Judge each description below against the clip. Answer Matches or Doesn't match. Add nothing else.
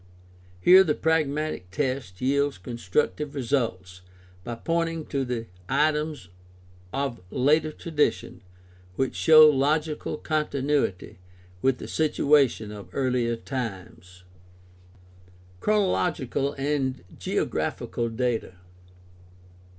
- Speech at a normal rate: Doesn't match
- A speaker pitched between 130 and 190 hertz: Matches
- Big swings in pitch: Doesn't match